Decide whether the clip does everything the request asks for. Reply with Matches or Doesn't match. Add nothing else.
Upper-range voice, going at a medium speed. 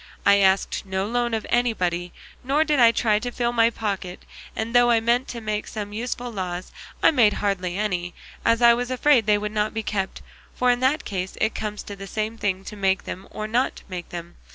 Doesn't match